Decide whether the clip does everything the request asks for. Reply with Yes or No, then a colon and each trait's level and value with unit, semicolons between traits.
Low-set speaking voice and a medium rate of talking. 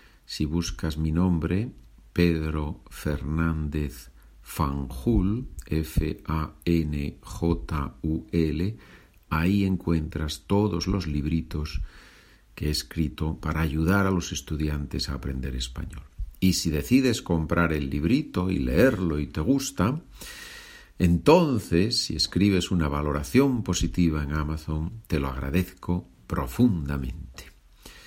No: very low, 80 Hz; slow, 100 wpm